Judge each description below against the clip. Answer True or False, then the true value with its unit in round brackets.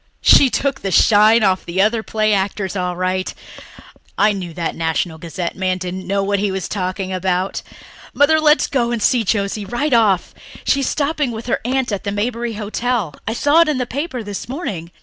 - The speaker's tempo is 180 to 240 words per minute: True (200 wpm)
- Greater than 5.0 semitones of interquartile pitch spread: False (4.6 semitones)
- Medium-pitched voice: False (205 Hz)